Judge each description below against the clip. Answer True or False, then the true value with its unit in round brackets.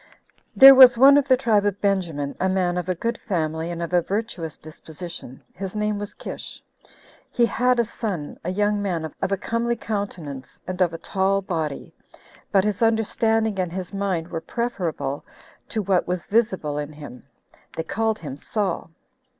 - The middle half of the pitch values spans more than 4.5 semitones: True (4.9 semitones)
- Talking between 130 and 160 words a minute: False (180 wpm)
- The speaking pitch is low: False (190 Hz)